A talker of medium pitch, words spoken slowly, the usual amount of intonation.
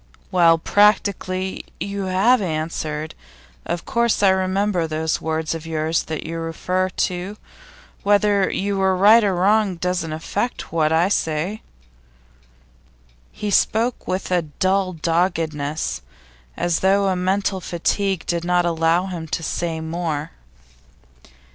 Yes: medium, 180 Hz; slow, 125 wpm; average, 3.2 semitones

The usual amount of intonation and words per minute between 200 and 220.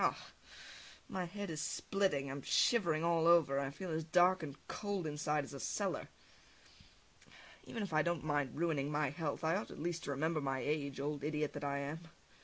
Yes: average, 3.2 semitones; fast, 205 wpm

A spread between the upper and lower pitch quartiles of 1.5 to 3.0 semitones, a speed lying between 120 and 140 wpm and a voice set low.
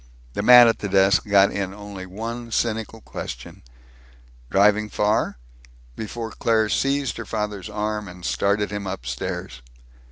Yes: narrow, 2.4 semitones; slow, 135 wpm; low, 105 Hz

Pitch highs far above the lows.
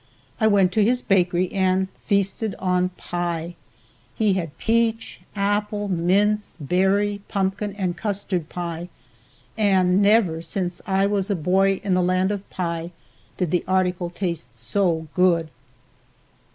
No: narrow, 2.4 semitones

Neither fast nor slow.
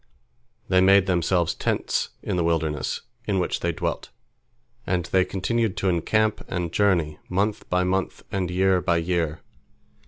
Yes: average, 150 wpm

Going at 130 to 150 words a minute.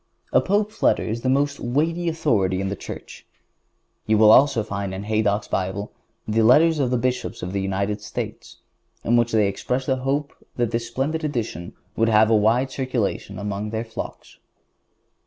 No: average, 175 wpm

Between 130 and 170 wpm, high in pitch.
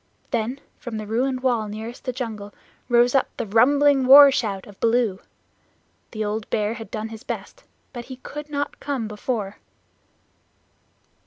Yes: average, 155 wpm; high, 235 Hz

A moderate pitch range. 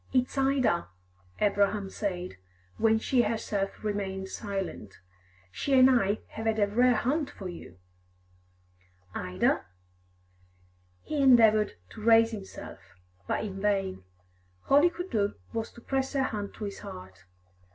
Yes: average, 4.2 semitones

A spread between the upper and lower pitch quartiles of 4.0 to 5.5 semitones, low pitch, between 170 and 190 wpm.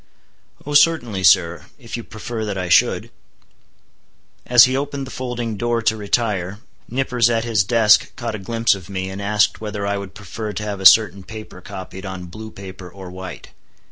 No: average, 3.5 semitones; low, 105 Hz; average, 185 wpm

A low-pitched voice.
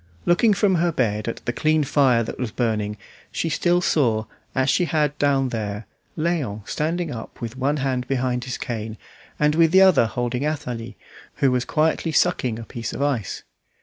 Yes: low, 130 Hz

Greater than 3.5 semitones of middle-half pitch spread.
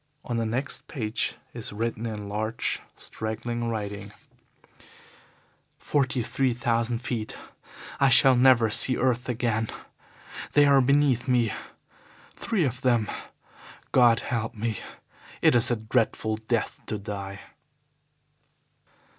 No: narrow, 2.5 semitones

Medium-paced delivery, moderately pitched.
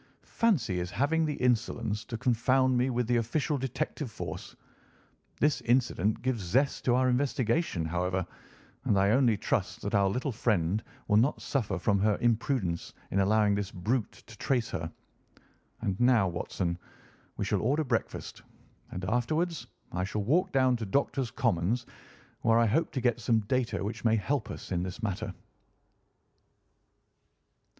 No: average, 155 wpm; low, 115 Hz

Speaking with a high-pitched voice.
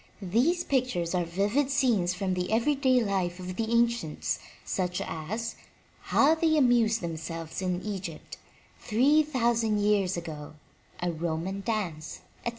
Yes: high, 205 Hz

